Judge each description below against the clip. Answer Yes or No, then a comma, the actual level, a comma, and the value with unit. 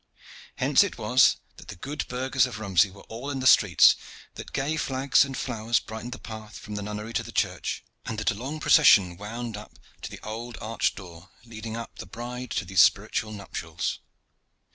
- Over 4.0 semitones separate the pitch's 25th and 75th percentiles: No, average, 3.3 semitones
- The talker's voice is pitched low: Yes, low, 115 Hz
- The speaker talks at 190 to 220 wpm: Yes, average, 195 wpm